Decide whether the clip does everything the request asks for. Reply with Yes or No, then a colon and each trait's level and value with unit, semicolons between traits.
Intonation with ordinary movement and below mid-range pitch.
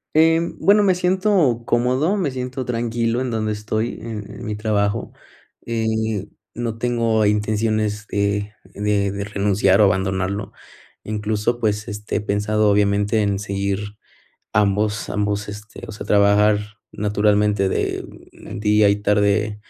No: narrow, 2.0 semitones; low, 105 Hz